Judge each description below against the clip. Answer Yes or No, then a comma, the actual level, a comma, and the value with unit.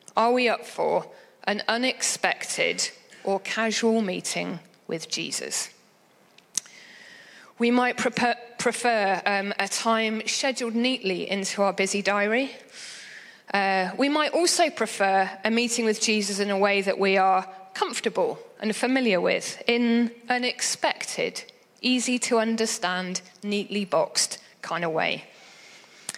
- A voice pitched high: Yes, high, 225 Hz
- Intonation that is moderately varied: Yes, average, 4.0 semitones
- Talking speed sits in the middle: No, slow, 120 wpm